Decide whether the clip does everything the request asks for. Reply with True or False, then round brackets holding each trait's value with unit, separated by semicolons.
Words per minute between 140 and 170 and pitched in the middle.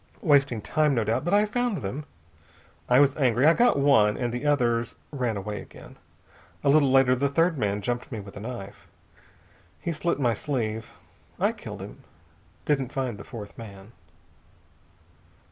False (165 wpm; 125 Hz)